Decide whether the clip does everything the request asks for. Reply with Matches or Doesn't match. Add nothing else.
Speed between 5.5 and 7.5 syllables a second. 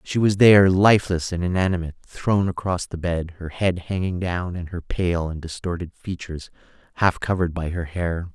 Doesn't match